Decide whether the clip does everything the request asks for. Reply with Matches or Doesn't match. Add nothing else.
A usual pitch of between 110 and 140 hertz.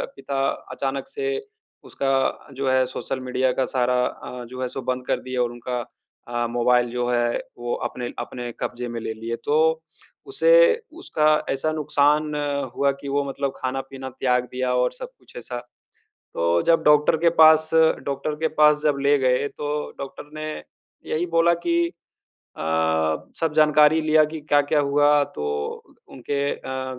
Matches